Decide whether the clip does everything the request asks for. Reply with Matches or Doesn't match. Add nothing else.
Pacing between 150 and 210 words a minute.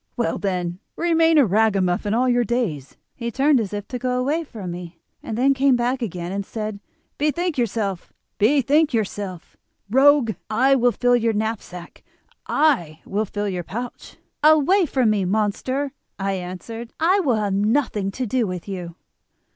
Matches